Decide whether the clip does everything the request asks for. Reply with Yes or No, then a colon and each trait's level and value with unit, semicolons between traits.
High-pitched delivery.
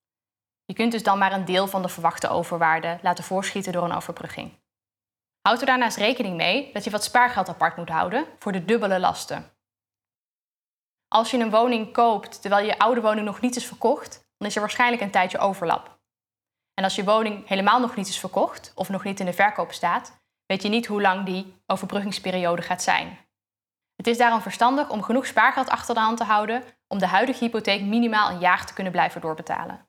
Yes: high, 200 Hz